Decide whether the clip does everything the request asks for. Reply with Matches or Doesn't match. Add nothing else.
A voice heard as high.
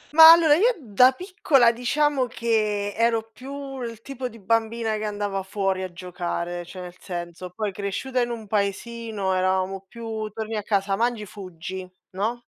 Matches